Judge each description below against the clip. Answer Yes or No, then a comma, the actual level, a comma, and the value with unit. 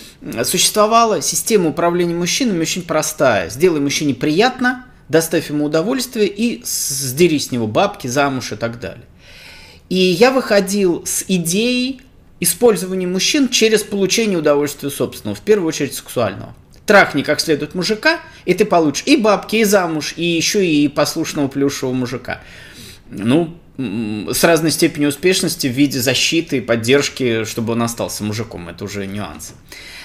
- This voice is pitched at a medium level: Yes, medium, 160 Hz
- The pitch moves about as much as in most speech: No, wide, 6.5 semitones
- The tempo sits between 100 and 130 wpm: No, average, 140 wpm